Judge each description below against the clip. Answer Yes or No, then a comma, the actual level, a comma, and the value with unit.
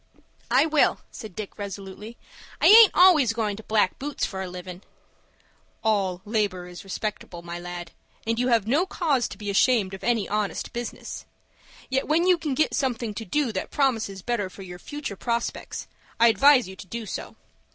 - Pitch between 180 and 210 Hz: No, high, 220 Hz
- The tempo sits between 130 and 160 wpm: No, average, 185 wpm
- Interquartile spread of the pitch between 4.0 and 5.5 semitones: Yes, average, 5.2 semitones